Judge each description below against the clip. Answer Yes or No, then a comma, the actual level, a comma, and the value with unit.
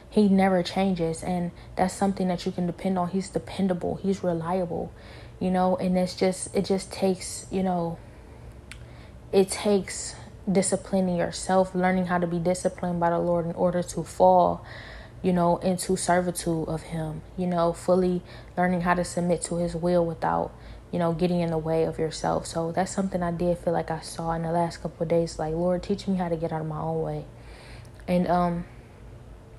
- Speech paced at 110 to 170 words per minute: No, average, 195 wpm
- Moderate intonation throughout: No, narrow, 1.9 semitones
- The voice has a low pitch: No, medium, 175 Hz